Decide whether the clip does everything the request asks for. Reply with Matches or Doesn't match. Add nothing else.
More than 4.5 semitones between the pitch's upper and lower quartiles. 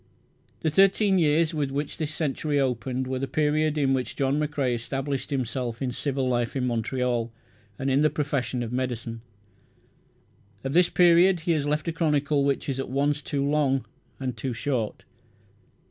Doesn't match